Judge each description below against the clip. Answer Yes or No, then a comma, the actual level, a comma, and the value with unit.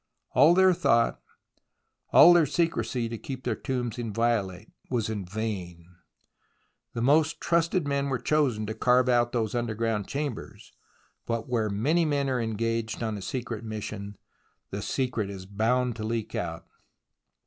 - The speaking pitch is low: Yes, low, 115 Hz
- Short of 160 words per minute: Yes, average, 150 wpm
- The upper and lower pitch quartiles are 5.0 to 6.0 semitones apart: No, average, 3.5 semitones